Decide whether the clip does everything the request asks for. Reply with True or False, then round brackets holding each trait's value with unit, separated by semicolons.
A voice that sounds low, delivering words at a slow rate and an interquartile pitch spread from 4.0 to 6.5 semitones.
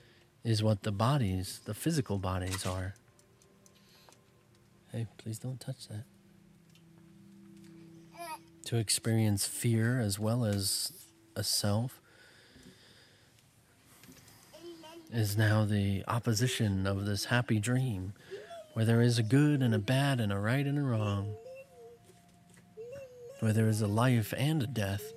True (120 Hz; 120 wpm; 5.6 semitones)